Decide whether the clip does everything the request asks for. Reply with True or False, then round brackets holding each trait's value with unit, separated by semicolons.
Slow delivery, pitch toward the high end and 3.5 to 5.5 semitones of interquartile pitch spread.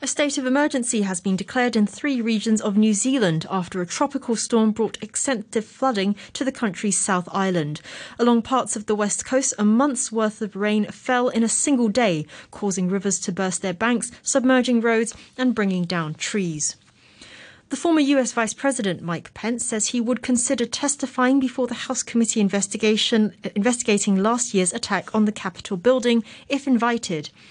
False (175 wpm; 225 Hz; 4.0 semitones)